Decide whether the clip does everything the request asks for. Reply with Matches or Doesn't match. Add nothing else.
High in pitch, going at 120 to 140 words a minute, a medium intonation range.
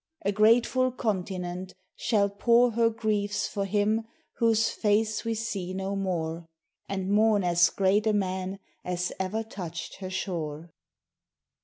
Matches